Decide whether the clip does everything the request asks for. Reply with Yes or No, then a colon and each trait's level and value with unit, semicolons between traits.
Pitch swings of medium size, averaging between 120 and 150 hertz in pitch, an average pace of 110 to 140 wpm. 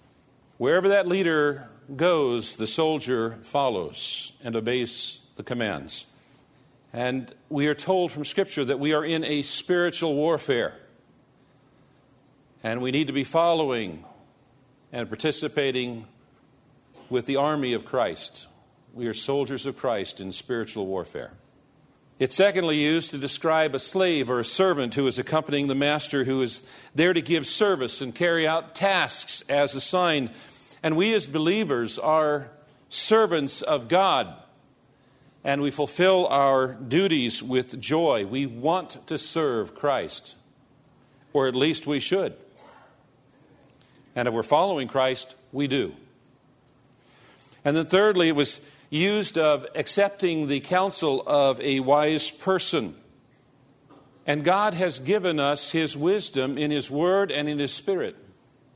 Yes: average, 3.3 semitones; medium, 140 Hz; slow, 135 wpm